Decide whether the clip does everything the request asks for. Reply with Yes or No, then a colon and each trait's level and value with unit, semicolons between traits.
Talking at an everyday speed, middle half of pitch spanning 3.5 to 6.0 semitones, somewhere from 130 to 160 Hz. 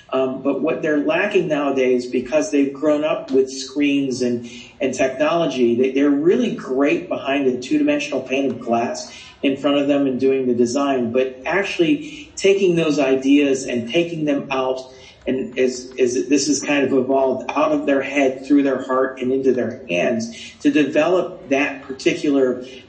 No: average, 175 wpm; narrow, 2.5 semitones; low, 135 Hz